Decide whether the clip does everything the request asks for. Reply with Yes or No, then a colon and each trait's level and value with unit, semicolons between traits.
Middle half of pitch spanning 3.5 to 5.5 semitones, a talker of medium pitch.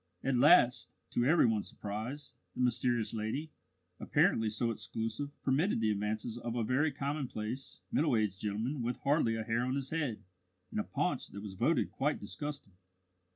No: average, 4.1 semitones; low, 120 Hz